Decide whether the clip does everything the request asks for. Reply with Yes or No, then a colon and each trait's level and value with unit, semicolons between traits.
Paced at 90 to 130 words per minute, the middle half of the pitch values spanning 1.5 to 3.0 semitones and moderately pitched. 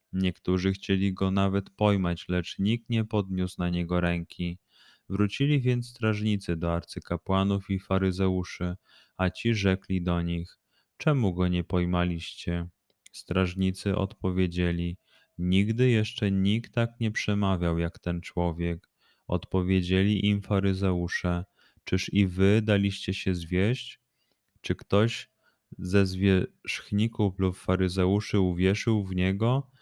No: average, 115 wpm; narrow, 2.5 semitones; very low, 95 Hz